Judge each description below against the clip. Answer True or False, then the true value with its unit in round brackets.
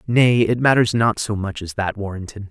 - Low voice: True (105 Hz)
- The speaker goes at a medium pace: False (215 wpm)